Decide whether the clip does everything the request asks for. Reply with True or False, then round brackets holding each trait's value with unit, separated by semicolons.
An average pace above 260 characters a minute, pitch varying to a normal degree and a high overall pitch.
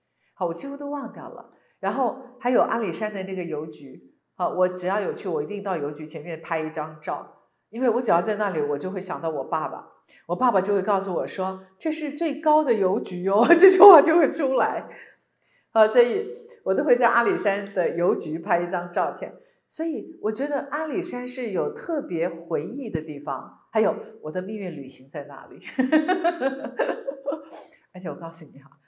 False (270 characters per minute; 8.6 semitones; 200 Hz)